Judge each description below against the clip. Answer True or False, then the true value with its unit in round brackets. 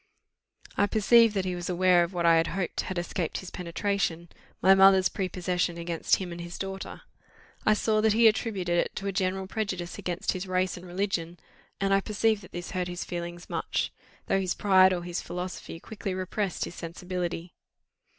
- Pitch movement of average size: False (2.0 semitones)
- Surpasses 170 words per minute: True (190 wpm)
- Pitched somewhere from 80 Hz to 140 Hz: False (185 Hz)